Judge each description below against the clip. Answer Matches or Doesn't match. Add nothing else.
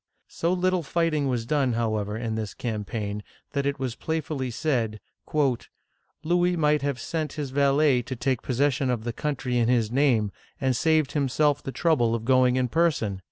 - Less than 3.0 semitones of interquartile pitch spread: Doesn't match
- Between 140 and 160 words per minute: Doesn't match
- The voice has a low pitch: Matches